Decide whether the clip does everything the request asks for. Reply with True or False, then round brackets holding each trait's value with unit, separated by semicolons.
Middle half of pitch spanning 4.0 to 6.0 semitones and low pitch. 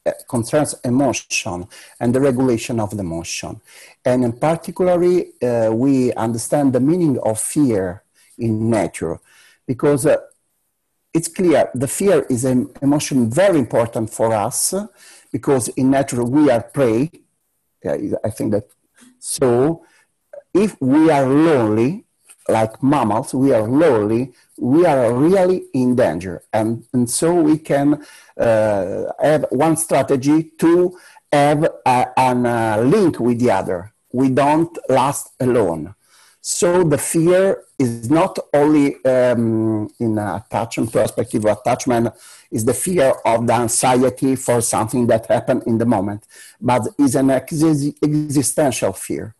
True (4.7 semitones; 130 Hz)